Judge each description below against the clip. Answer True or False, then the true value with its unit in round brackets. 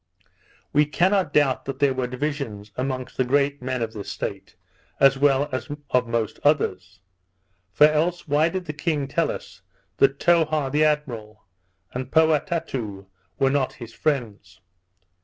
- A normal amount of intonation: True (3.7 semitones)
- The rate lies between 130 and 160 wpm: True (150 wpm)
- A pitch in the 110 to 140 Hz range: True (135 Hz)